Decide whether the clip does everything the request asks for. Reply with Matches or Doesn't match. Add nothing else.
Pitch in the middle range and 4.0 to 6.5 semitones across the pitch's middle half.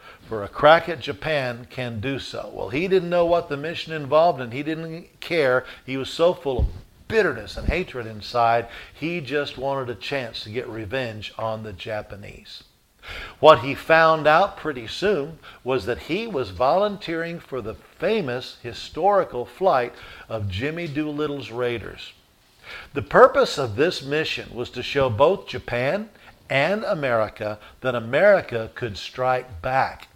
Doesn't match